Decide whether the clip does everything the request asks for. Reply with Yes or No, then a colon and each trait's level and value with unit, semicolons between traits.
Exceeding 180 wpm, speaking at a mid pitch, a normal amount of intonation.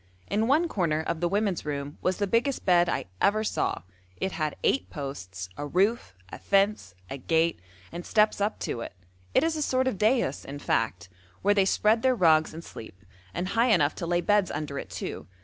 No: fast, 205 wpm; medium, 180 Hz; wide, 6.4 semitones